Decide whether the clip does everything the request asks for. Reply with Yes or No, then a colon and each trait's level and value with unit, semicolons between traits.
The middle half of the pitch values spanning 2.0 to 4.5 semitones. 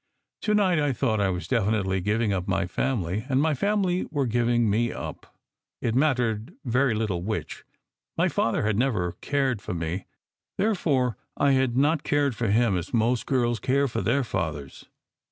No: average, 5.0 semitones